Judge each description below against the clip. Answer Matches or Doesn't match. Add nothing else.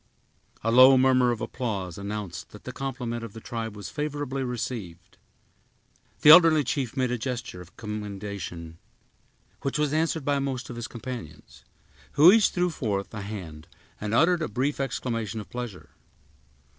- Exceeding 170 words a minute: Doesn't match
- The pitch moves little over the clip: Doesn't match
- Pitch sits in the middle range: Doesn't match